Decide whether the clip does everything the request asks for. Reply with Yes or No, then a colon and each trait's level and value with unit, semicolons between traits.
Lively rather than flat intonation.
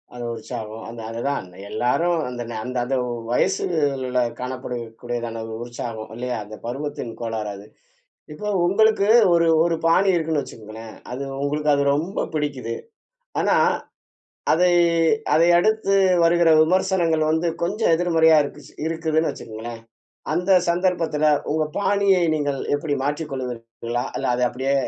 Yes: wide, 5.8 semitones